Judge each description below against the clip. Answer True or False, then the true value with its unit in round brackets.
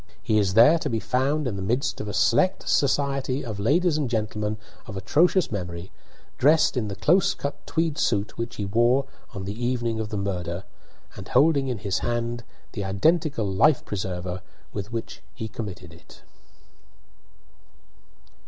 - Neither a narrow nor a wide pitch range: False (5.9 semitones)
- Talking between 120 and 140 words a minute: False (160 wpm)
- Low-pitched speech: True (115 Hz)